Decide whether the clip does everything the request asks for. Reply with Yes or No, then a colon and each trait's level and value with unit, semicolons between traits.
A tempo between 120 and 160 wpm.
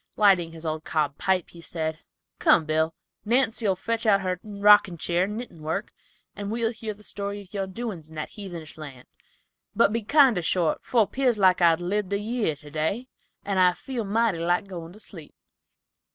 No: average, 185 wpm